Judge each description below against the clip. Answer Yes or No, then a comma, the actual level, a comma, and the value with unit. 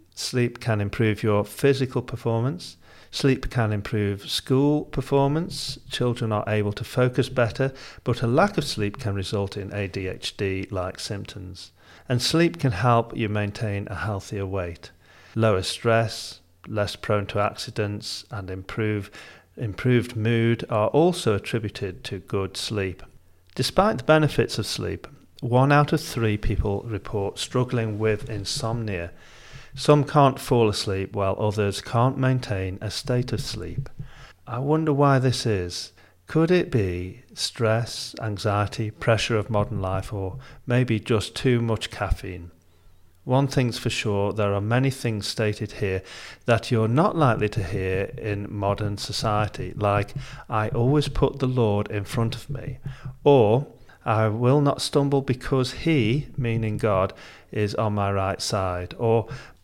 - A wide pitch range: No, average, 4.3 semitones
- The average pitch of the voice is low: Yes, low, 110 Hz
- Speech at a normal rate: Yes, average, 145 wpm